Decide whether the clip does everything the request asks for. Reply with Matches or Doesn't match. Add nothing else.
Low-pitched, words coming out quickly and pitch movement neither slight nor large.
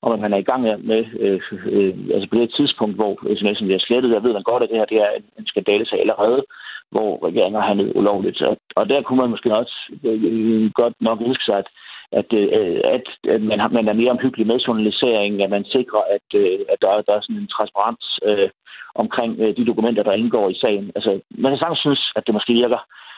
Doesn't match